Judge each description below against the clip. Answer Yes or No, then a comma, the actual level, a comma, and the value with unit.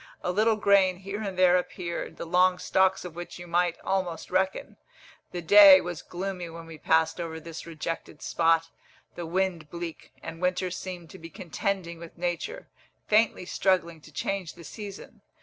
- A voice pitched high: No, medium, 180 Hz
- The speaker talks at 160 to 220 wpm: Yes, average, 170 wpm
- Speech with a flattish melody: Yes, narrow, 2.2 semitones